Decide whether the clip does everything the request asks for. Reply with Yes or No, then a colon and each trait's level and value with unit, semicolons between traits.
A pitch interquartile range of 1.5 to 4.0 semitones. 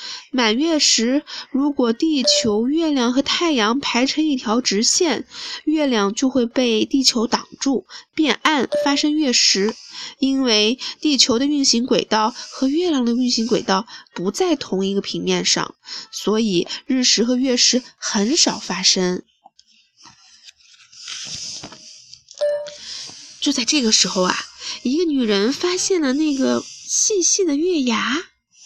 No: average, 5.2 semitones